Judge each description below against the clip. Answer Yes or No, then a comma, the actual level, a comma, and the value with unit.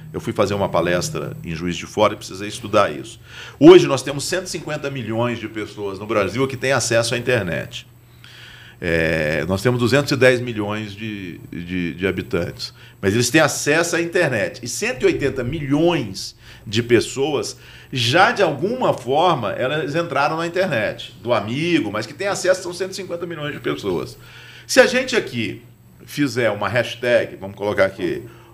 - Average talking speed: Yes, average, 160 wpm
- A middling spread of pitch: No, wide, 6.1 semitones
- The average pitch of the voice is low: Yes, low, 120 Hz